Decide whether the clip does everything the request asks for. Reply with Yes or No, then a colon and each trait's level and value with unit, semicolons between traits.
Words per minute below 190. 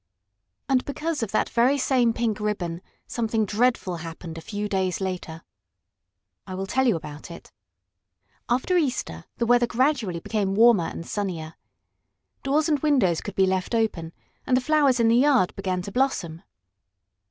Yes: average, 160 wpm